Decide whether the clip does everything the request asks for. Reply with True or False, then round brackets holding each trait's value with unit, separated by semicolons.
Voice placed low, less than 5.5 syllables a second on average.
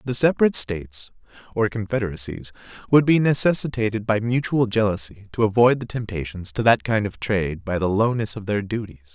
False (105 Hz; 5.7 syllables/s)